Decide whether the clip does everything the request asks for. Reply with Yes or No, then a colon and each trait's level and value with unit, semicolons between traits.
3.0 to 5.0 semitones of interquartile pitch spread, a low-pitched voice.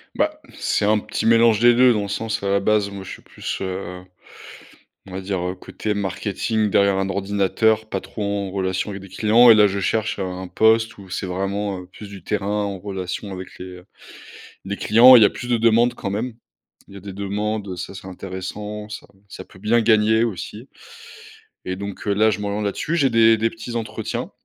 No: narrow, 2.4 semitones; low, 100 Hz